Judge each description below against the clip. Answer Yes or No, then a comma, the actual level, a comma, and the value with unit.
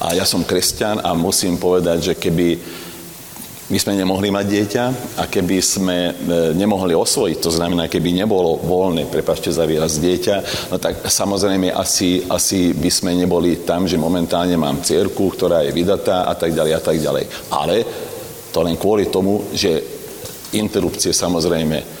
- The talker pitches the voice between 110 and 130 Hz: No, very low, 90 Hz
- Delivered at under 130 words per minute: No, average, 160 wpm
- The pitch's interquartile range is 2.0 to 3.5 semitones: Yes, average, 2.7 semitones